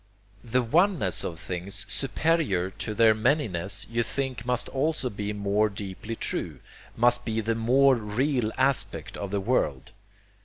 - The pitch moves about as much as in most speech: Yes, average, 4.5 semitones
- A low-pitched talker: Yes, low, 115 Hz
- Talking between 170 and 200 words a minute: No, average, 145 wpm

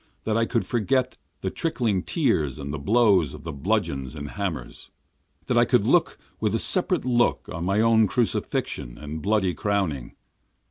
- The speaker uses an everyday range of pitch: No, wide, 7.5 semitones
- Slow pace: No, average, 170 wpm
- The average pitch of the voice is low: Yes, low, 100 Hz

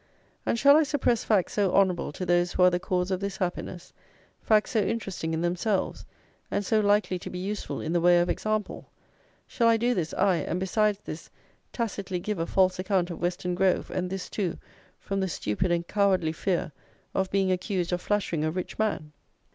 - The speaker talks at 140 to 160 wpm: No, average, 200 wpm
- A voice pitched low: No, medium, 185 Hz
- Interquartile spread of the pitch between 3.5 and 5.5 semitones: No, average, 2.8 semitones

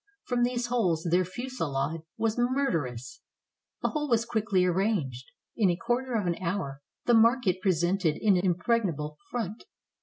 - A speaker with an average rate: Yes, average, 150 wpm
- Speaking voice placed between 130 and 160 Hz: No, high, 195 Hz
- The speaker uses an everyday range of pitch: No, wide, 6.2 semitones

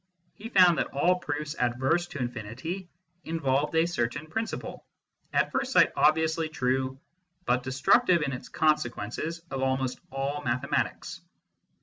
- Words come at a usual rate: No, slow, 130 wpm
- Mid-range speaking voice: Yes, medium, 145 Hz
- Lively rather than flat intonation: No, average, 4.1 semitones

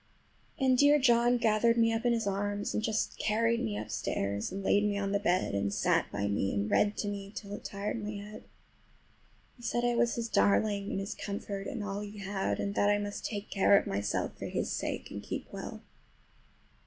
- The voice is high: Yes, high, 205 Hz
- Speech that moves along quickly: Yes, fast, 215 wpm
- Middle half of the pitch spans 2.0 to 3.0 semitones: Yes, narrow, 2.5 semitones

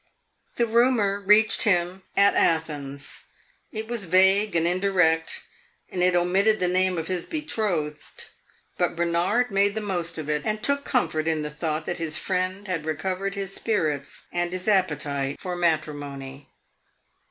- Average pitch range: Yes, average, 4.0 semitones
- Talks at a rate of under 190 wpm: Yes, average, 155 wpm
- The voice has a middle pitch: Yes, medium, 180 Hz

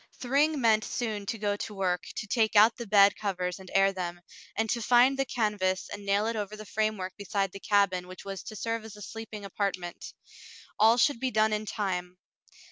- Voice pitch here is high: Yes, high, 210 Hz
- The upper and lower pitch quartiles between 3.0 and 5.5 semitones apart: No, narrow, 2.5 semitones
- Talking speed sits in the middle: No, fast, 210 wpm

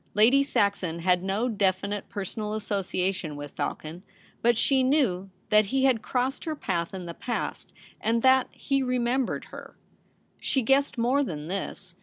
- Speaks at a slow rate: No, average, 160 wpm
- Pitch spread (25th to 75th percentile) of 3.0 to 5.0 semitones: No, wide, 5.6 semitones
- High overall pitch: Yes, high, 215 Hz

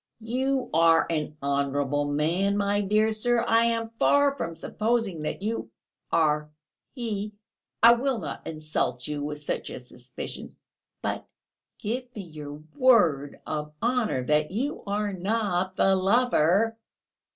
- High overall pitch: Yes, high, 195 Hz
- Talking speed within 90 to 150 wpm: Yes, slow, 135 wpm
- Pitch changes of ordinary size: No, wide, 7.1 semitones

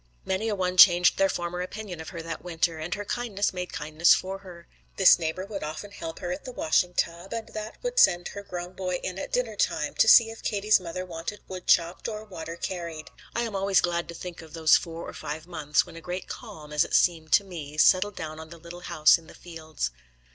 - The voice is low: No, medium, 180 Hz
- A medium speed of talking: No, fast, 235 wpm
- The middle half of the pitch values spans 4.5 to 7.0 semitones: No, average, 3.1 semitones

